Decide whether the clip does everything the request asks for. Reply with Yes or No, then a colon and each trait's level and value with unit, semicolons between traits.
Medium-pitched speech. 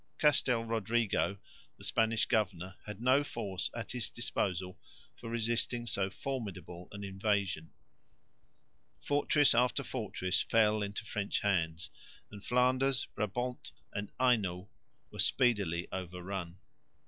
No: low, 105 Hz